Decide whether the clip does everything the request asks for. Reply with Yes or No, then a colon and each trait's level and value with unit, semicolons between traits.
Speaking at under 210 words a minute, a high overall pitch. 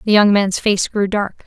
No: fast, 245 wpm; high, 200 Hz